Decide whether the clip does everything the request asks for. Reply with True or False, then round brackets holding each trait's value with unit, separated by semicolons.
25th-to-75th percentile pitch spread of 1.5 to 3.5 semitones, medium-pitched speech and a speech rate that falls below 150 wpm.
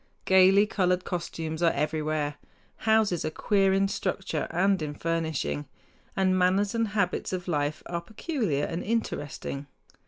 False (4.0 semitones; 180 Hz; 135 wpm)